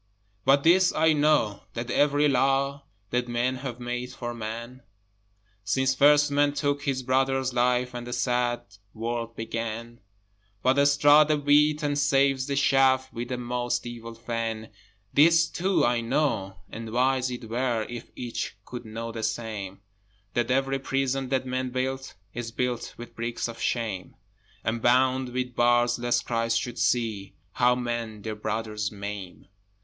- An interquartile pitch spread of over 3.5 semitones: No, narrow, 2.6 semitones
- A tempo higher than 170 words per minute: No, average, 155 wpm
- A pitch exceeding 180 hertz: No, low, 125 Hz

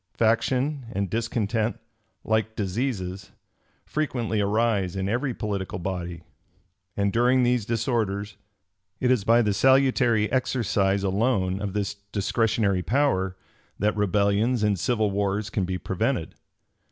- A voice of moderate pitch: No, low, 105 Hz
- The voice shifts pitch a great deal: No, average, 3.3 semitones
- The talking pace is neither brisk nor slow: No, slow, 120 wpm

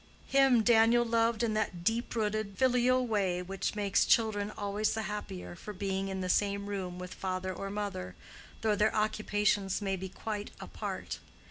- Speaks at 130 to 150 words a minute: No, average, 165 wpm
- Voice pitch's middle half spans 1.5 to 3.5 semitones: Yes, narrow, 2.5 semitones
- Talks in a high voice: Yes, high, 205 Hz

